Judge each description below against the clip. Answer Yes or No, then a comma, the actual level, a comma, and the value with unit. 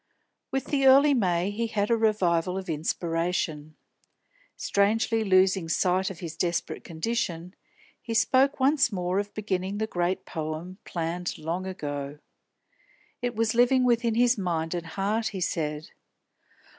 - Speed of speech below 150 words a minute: Yes, average, 140 wpm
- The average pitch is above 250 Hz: No, high, 190 Hz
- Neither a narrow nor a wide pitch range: Yes, average, 4.9 semitones